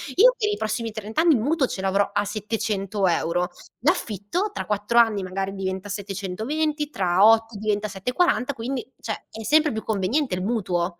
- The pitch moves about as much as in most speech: Yes, average, 4.4 semitones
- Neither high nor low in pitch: No, high, 215 Hz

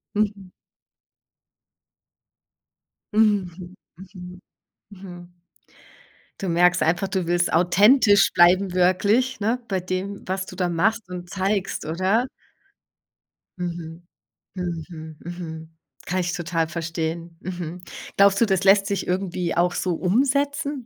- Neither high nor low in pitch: Yes, medium, 180 Hz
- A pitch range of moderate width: No, narrow, 2.3 semitones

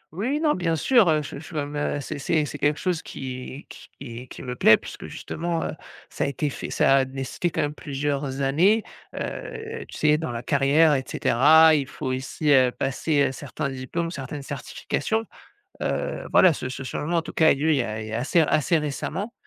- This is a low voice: No, medium, 145 Hz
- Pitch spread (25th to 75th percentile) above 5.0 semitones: No, average, 3.4 semitones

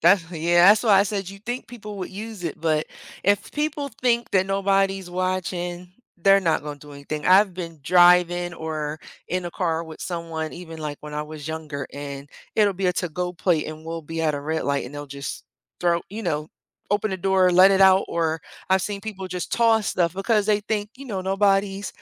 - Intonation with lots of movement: No, average, 3.6 semitones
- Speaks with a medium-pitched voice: Yes, medium, 180 Hz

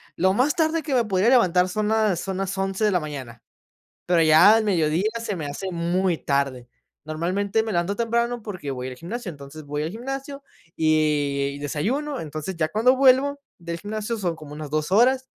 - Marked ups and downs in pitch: Yes, wide, 6.4 semitones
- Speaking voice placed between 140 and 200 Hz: Yes, medium, 185 Hz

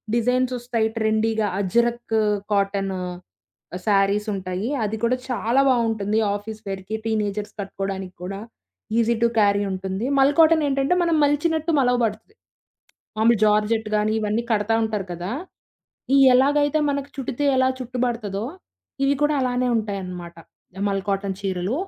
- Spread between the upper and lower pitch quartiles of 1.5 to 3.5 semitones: No, average, 4.0 semitones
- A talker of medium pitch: No, high, 220 Hz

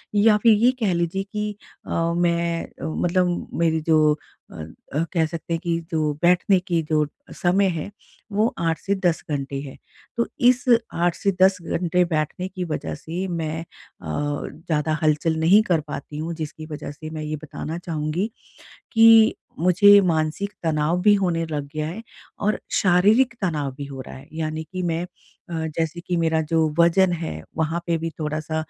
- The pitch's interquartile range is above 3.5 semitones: No, average, 2.9 semitones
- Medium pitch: Yes, medium, 165 Hz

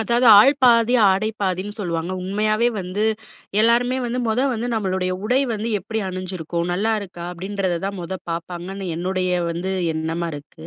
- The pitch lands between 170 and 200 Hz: Yes, high, 190 Hz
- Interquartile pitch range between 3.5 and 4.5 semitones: Yes, average, 3.8 semitones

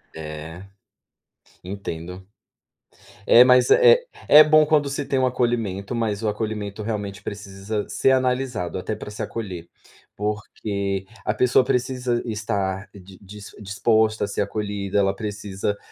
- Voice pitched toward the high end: No, low, 105 Hz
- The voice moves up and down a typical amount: Yes, average, 3.7 semitones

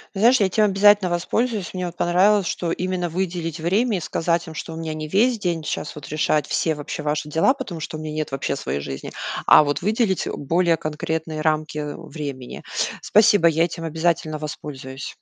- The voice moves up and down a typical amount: Yes, average, 3.6 semitones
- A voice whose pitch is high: No, medium, 165 Hz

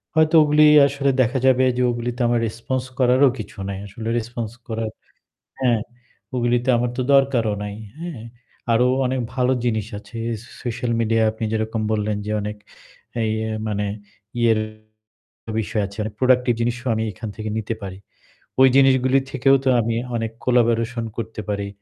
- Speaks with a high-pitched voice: No, low, 120 Hz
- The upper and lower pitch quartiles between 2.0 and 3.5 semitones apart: Yes, average, 2.7 semitones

